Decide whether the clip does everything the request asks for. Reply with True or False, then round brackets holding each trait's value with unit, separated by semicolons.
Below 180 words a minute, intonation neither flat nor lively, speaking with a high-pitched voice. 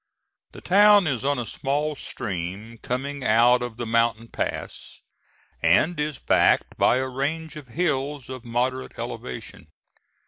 False (140 wpm; 4.1 semitones; 130 Hz)